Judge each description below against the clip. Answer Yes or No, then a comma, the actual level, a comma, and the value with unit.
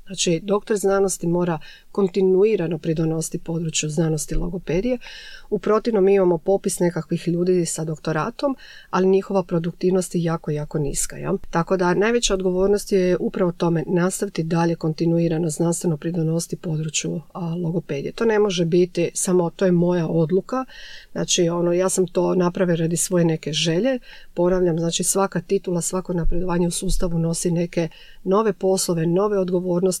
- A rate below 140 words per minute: No, average, 145 wpm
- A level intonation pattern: Yes, narrow, 2.3 semitones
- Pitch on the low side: No, medium, 175 Hz